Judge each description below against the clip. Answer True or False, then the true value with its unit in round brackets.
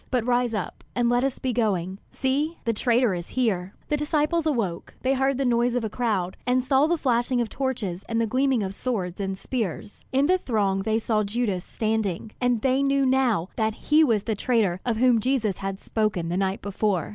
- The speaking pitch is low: False (230 Hz)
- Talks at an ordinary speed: False (210 wpm)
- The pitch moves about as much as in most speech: True (4.4 semitones)